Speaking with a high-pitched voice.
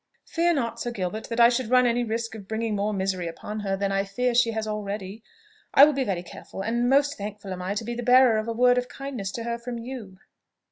Yes: high, 230 Hz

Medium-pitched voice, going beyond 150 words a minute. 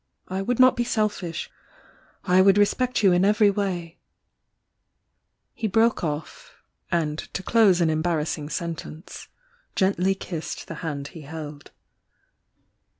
No: medium, 180 Hz; average, 145 wpm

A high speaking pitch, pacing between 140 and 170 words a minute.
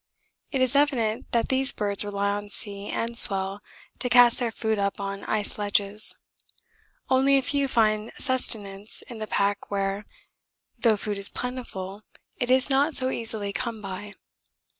Yes: high, 215 Hz; average, 160 wpm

